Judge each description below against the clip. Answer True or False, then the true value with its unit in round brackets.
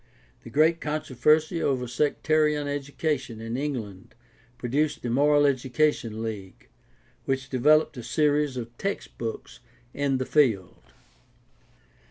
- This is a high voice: False (135 Hz)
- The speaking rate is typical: False (110 wpm)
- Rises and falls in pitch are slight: False (4.0 semitones)